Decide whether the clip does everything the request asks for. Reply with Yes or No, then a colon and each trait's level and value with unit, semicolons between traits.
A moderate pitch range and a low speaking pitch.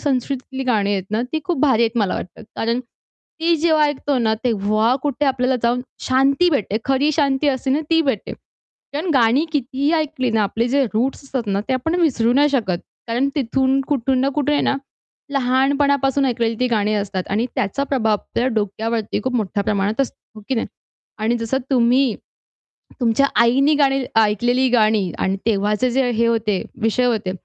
No: average, 3.7 semitones; very high, 250 Hz